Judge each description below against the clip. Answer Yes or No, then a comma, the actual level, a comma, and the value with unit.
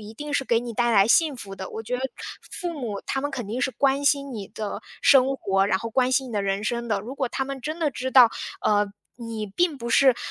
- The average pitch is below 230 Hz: No, high, 245 Hz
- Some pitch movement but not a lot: Yes, average, 4.1 semitones